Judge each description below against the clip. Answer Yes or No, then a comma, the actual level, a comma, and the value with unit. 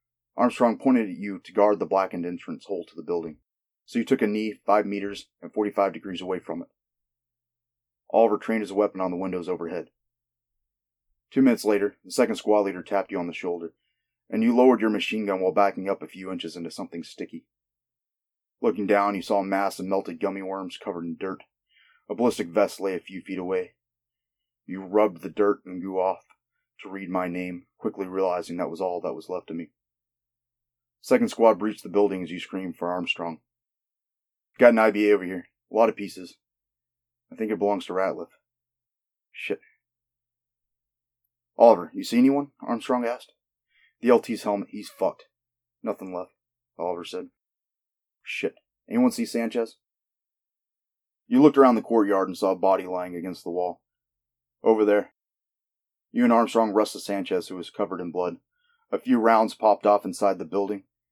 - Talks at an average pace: Yes, average, 180 wpm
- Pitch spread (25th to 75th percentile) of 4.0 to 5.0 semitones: Yes, average, 4.6 semitones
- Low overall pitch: Yes, low, 100 Hz